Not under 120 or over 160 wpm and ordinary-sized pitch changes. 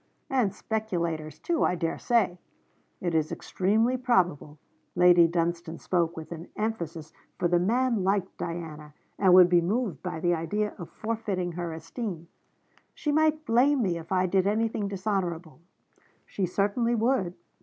Yes: average, 150 wpm; average, 4.6 semitones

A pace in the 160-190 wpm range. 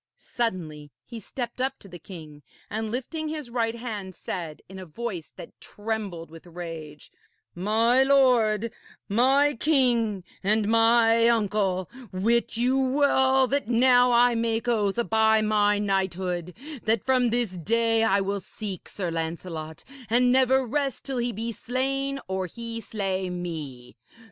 No: average, 145 wpm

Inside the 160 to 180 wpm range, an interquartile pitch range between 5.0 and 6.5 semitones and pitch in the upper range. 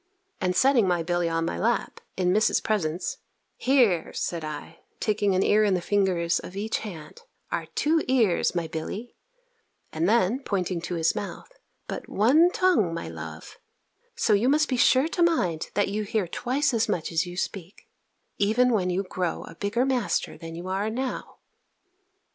Yes: average, 175 wpm; wide, 5.6 semitones; high, 195 Hz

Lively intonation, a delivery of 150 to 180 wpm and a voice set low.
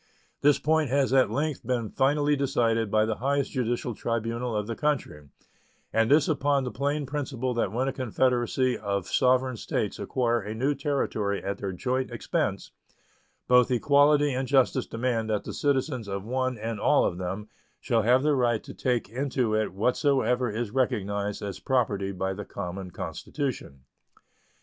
No: average, 3.9 semitones; average, 165 wpm; low, 125 Hz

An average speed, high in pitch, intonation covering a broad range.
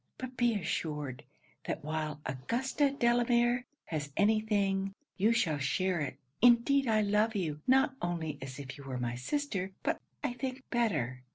Yes: average, 160 wpm; high, 195 Hz; wide, 8.3 semitones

